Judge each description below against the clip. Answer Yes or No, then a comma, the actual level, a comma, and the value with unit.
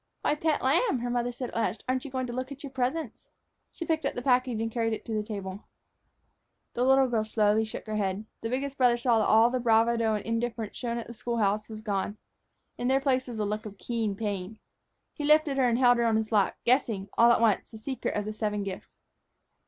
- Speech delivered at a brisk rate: Yes, fast, 240 wpm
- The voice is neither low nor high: No, high, 235 Hz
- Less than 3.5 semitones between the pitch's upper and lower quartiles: Yes, average, 3.0 semitones